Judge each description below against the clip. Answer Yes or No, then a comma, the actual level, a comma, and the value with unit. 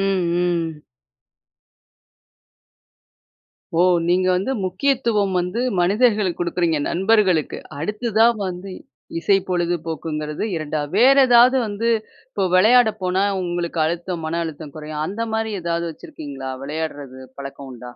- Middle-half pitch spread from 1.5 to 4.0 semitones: No, average, 4.5 semitones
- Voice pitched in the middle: Yes, medium, 175 Hz